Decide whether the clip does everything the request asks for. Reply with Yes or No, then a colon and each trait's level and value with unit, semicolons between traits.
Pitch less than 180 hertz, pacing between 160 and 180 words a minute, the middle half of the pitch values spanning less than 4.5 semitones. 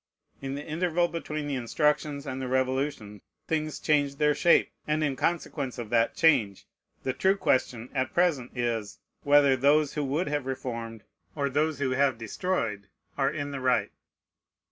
Yes: medium, 140 Hz; average, 165 wpm; average, 3.1 semitones